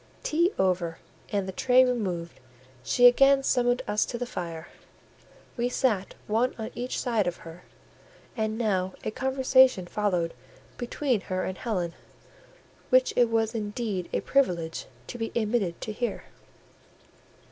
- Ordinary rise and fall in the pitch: Yes, average, 5.0 semitones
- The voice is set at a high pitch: Yes, high, 220 Hz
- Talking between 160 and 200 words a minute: No, average, 140 wpm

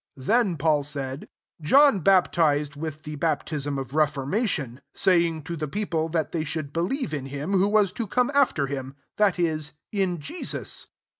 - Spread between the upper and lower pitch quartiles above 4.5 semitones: Yes, average, 5.0 semitones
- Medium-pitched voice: Yes, medium, 160 Hz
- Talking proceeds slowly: No, average, 175 wpm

